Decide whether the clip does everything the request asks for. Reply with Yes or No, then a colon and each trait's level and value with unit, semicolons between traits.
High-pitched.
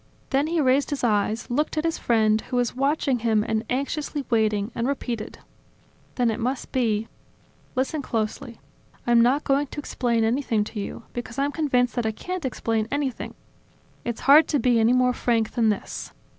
Yes: high, 245 Hz